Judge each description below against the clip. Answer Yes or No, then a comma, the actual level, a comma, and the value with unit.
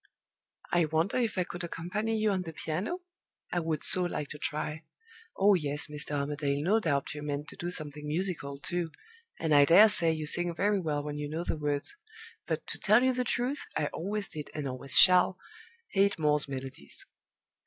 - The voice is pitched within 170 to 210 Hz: No, medium, 160 Hz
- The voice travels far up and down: No, average, 4.3 semitones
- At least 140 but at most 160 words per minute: No, average, 195 wpm